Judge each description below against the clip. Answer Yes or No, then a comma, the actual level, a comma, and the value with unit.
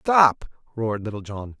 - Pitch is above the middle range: No, low, 120 Hz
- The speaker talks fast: No, average, 150 wpm